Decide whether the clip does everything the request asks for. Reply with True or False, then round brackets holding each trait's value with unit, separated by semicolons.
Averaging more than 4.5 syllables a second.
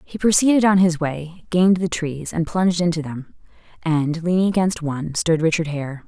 True (5.1 syllables/s)